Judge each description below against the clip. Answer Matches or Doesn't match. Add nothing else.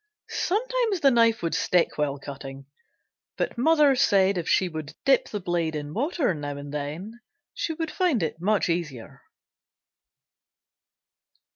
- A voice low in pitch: Doesn't match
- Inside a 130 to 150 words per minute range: Matches